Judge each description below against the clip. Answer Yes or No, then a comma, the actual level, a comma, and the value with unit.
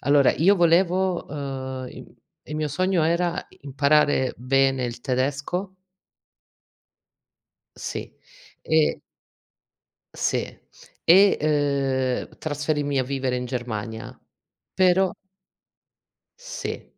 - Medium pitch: Yes, medium, 145 Hz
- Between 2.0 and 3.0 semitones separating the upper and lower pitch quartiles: No, average, 4.5 semitones